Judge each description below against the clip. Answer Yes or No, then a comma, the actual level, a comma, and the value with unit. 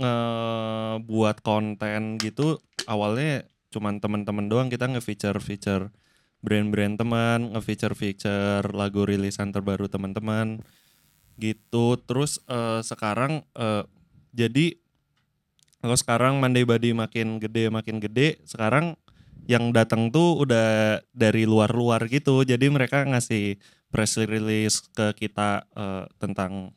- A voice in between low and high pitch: No, low, 110 Hz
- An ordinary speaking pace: No, slow, 115 wpm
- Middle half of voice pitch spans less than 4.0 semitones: Yes, narrow, 2.4 semitones